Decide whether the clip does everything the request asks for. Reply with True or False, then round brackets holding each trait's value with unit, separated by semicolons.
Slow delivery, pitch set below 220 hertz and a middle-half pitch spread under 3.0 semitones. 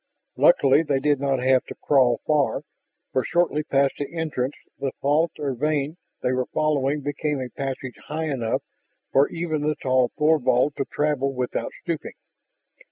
False (160 wpm; 140 Hz; 2.5 semitones)